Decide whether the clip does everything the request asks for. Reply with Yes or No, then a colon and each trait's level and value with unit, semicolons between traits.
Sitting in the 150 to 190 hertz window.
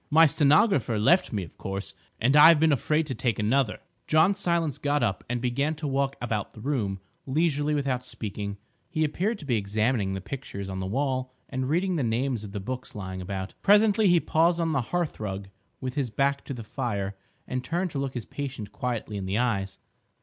No: low, 130 Hz